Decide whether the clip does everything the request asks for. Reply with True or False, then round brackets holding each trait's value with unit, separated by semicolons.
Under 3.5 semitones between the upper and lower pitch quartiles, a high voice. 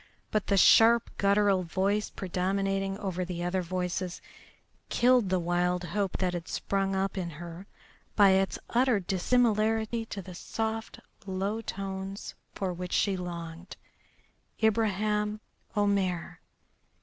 True (2.5 semitones; 195 Hz)